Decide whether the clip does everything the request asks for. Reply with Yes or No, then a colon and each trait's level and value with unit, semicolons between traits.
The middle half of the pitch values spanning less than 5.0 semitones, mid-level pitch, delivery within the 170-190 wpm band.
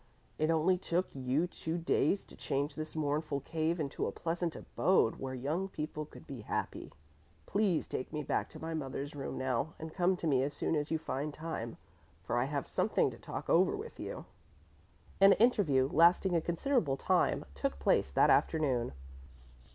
Yes: average, 3.8 semitones; medium, 155 Hz; average, 180 wpm